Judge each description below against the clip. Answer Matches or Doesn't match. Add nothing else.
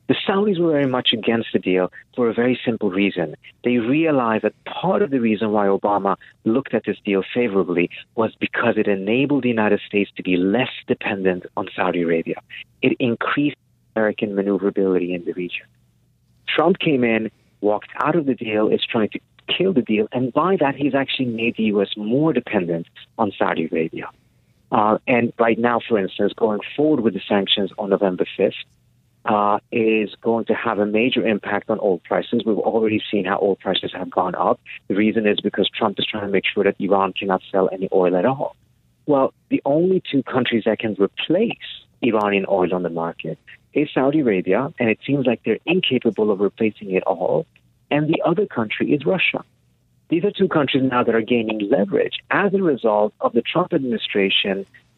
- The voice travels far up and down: Doesn't match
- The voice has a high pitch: Doesn't match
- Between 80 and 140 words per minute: Doesn't match